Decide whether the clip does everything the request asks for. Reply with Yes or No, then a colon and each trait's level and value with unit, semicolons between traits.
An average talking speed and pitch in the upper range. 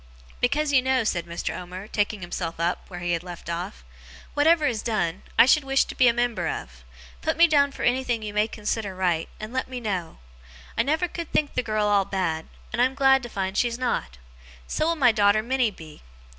No: fast, 220 wpm; high, 215 Hz